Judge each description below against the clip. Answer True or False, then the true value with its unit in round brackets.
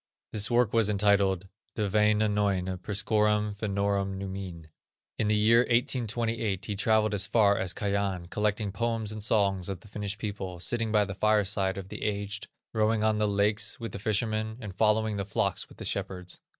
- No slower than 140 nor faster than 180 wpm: True (175 wpm)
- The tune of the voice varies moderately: False (1.6 semitones)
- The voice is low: True (105 Hz)